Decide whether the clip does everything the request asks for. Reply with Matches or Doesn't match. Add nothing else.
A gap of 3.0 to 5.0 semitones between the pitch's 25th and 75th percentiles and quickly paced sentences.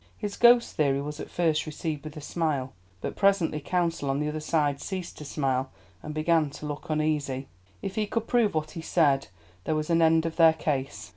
Doesn't match